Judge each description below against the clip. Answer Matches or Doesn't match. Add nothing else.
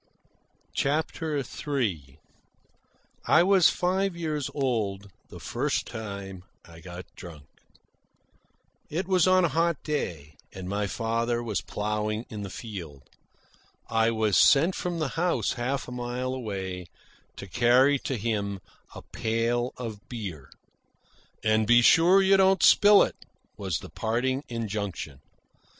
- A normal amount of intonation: Doesn't match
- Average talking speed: Doesn't match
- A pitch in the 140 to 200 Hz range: Doesn't match